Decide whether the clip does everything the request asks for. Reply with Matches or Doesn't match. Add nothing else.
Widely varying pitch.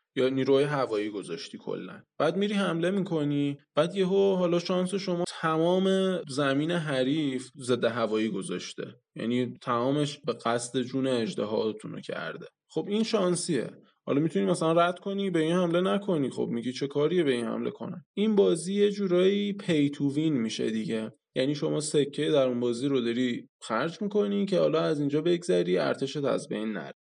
Matches